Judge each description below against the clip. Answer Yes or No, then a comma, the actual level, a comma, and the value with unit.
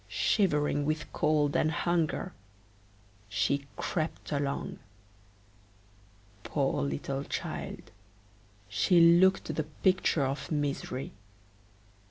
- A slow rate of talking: Yes, slow, 85 wpm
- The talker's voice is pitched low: No, medium, 150 Hz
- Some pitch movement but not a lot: Yes, average, 3.1 semitones